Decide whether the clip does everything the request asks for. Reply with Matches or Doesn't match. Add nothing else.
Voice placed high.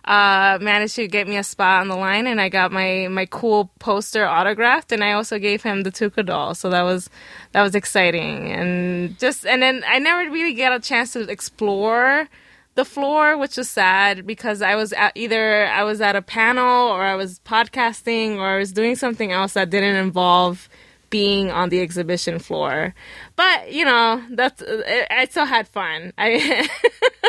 Matches